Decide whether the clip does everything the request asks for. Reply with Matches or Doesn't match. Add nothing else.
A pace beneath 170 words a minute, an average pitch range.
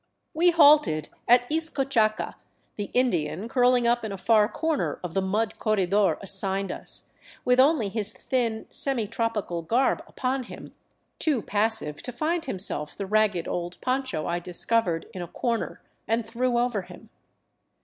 Matches